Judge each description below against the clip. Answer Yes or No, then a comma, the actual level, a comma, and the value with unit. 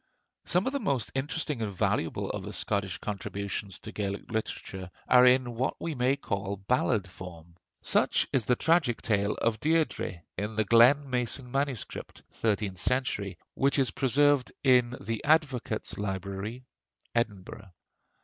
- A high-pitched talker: No, low, 115 Hz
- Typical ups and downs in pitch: Yes, average, 4.9 semitones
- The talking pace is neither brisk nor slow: Yes, average, 145 wpm